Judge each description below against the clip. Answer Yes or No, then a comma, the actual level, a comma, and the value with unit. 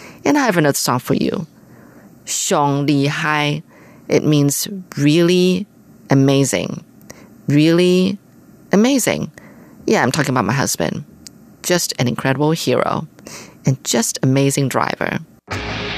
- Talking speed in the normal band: No, slow, 115 wpm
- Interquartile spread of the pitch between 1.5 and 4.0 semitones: No, average, 4.5 semitones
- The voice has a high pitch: No, medium, 145 Hz